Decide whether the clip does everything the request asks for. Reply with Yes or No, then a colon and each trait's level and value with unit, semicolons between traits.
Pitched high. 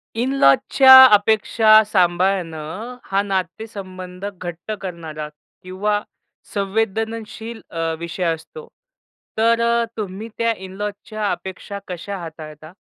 Yes: high, 195 Hz